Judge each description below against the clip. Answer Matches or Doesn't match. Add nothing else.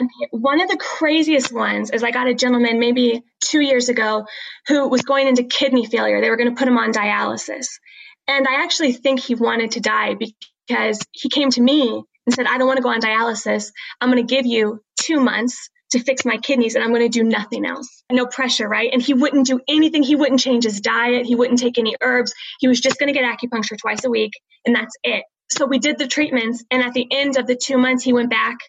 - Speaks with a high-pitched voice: Matches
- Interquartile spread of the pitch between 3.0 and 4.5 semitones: Doesn't match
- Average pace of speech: Doesn't match